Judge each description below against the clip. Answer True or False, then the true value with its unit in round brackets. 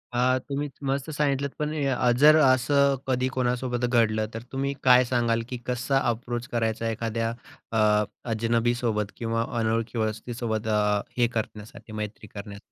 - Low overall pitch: True (120 Hz)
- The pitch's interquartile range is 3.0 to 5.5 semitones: False (2.5 semitones)